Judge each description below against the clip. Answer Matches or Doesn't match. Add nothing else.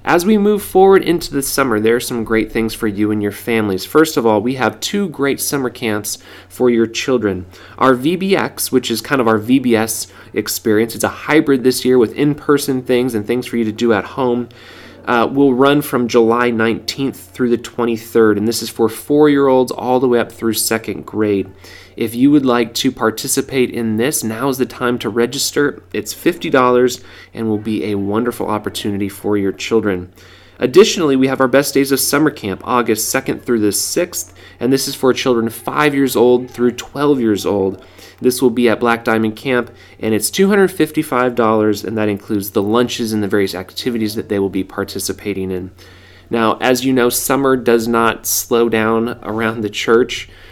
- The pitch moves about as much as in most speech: Matches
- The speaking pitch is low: Matches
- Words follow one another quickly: Doesn't match